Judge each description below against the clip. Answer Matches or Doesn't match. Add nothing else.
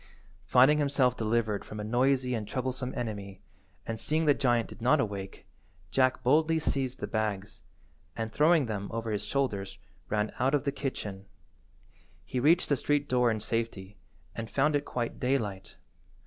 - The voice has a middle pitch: Doesn't match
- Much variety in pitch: Doesn't match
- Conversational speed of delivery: Matches